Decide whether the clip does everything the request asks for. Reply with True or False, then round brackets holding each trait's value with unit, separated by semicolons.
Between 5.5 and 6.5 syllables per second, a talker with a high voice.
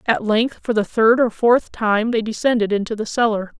False (5.0 syllables/s; 220 Hz)